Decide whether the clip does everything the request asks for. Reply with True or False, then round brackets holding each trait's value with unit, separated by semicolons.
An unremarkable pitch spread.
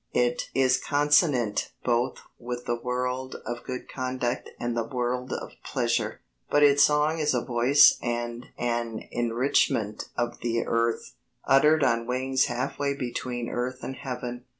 False (1.8 semitones)